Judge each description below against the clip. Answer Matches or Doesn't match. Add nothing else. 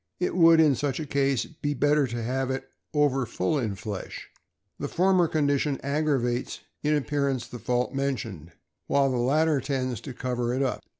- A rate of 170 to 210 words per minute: Matches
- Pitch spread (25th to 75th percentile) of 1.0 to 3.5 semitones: Matches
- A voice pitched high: Doesn't match